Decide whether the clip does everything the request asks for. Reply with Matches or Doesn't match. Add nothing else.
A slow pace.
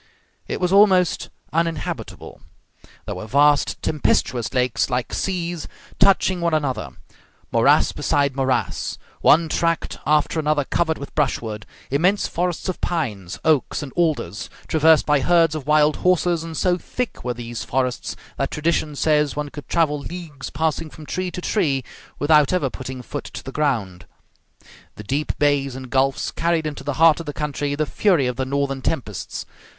Doesn't match